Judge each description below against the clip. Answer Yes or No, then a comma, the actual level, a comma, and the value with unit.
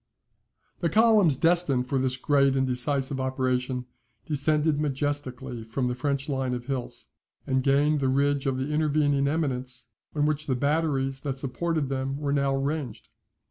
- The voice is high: No, medium, 140 Hz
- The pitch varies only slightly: Yes, narrow, 2.1 semitones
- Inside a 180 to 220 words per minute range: No, average, 155 wpm